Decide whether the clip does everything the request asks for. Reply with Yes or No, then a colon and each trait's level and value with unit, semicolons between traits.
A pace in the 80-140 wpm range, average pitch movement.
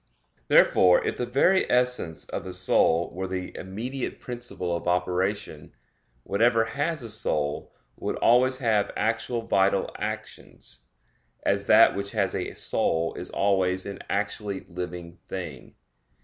Yes: slow, 135 wpm; average, 4.7 semitones